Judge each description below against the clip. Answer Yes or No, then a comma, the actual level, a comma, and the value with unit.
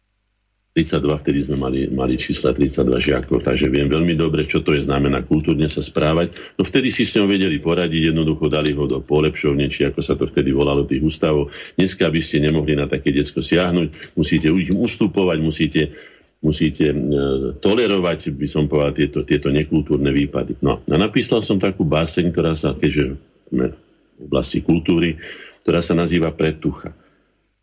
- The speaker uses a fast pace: Yes, fast, 170 wpm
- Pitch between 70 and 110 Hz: Yes, very low, 75 Hz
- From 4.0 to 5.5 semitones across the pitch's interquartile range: No, narrow, 2.4 semitones